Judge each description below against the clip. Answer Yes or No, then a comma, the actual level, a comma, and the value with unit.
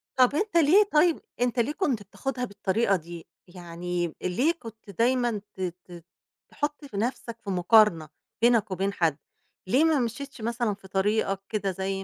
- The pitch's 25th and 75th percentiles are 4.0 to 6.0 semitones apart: Yes, average, 5.2 semitones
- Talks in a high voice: Yes, high, 215 Hz